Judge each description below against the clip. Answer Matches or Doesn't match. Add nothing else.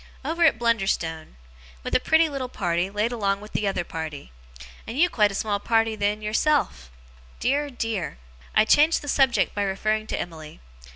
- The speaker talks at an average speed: Matches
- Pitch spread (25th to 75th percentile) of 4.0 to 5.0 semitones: Matches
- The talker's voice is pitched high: Matches